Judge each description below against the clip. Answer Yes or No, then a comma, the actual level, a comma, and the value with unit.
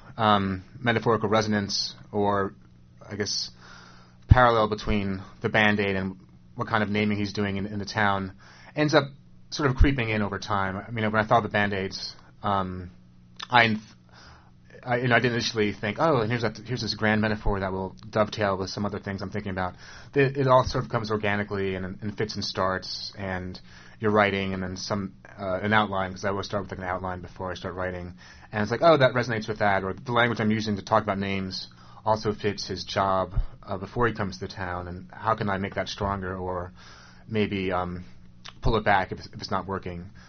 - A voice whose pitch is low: Yes, low, 100 Hz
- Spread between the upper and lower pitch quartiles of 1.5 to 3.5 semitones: Yes, average, 2.8 semitones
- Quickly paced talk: Yes, fast, 210 wpm